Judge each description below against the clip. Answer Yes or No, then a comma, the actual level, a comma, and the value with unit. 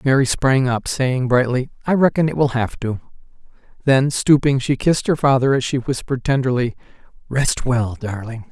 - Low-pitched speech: Yes, low, 130 Hz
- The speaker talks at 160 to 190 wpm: Yes, average, 170 wpm